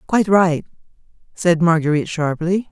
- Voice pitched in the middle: Yes, medium, 170 Hz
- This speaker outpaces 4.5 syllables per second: Yes, 5.3 syllables/s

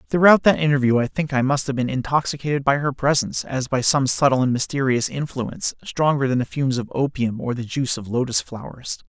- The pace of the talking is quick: Yes, fast, 210 wpm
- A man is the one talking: Yes, male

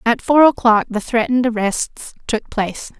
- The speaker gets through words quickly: No, average, 160 wpm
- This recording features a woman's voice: Yes, female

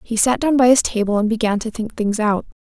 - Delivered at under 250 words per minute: No, fast, 270 wpm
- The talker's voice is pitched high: Yes, high, 225 Hz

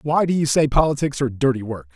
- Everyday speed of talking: No, fast, 245 wpm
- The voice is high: No, low, 135 Hz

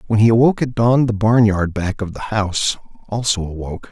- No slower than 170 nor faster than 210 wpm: Yes, average, 200 wpm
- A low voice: Yes, low, 105 Hz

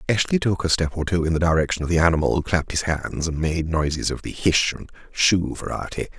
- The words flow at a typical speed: No, fast, 235 wpm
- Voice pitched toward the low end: Yes, very low, 85 Hz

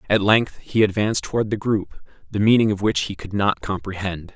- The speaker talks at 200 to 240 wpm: Yes, fast, 205 wpm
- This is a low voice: Yes, low, 100 Hz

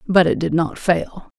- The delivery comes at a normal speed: No, fast, 215 wpm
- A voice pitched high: No, medium, 175 Hz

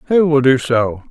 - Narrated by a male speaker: Yes, male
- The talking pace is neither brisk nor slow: No, fast, 220 wpm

